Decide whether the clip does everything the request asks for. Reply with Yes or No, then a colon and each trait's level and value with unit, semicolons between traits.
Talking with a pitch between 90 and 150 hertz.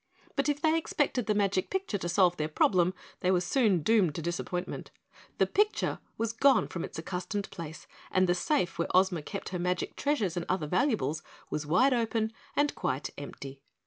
No: medium, 185 Hz